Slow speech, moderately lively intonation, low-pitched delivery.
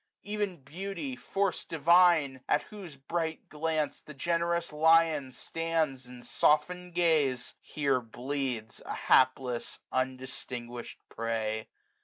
No: slow, 110 wpm; average, 4.6 semitones; medium, 150 Hz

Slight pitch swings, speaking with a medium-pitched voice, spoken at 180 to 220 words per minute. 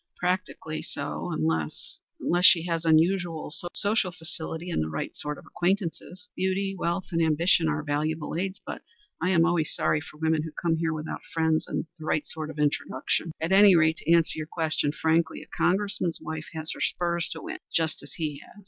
Yes: narrow, 2.2 semitones; medium, 165 Hz; average, 195 wpm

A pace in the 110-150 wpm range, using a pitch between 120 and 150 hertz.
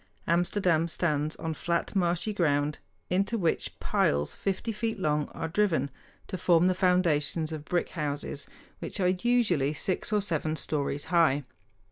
No: average, 145 wpm; medium, 170 Hz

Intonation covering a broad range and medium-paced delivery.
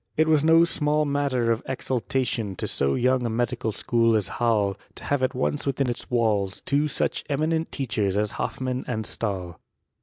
No: average, 4.4 semitones; average, 180 wpm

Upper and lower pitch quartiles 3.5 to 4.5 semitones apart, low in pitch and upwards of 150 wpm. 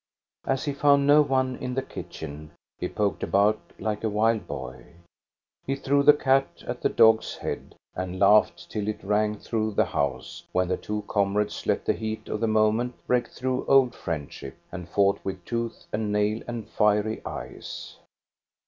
Yes: average, 3.8 semitones; low, 110 Hz; average, 175 wpm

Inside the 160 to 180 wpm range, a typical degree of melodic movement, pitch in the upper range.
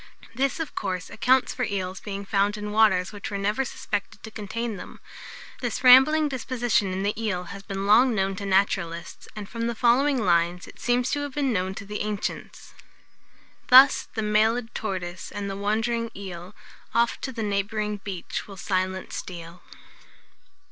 Yes: average, 170 wpm; average, 3.5 semitones; high, 210 Hz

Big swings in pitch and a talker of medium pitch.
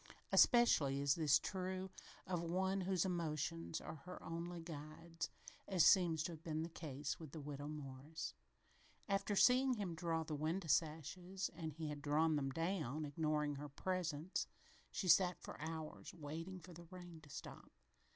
No: average, 3.1 semitones; medium, 165 Hz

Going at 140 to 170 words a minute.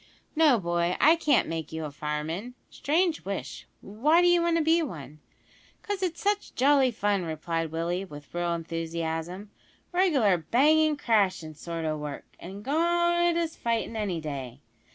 Yes: average, 155 wpm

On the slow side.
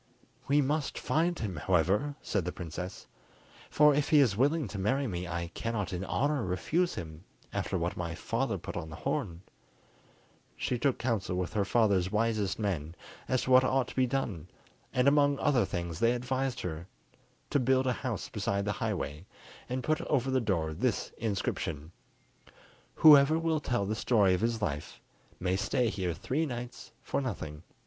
No: average, 170 wpm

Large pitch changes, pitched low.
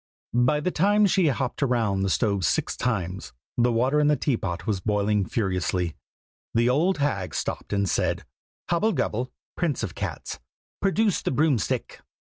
Yes: wide, 7.0 semitones; low, 120 Hz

